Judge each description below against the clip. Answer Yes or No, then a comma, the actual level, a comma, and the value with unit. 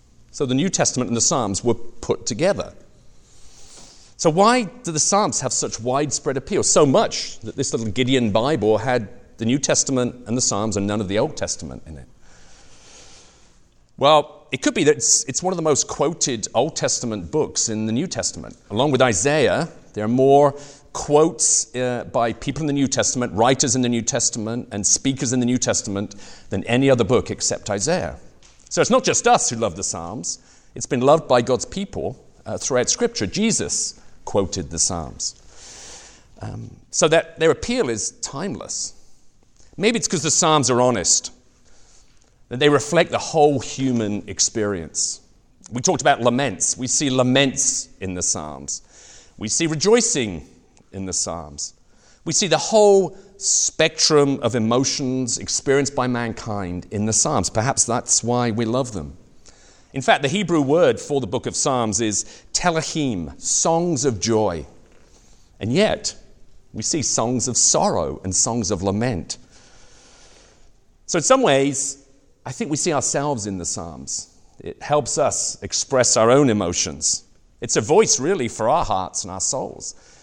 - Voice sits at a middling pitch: No, low, 125 Hz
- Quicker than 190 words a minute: No, average, 170 wpm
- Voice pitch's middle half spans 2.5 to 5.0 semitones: No, wide, 5.4 semitones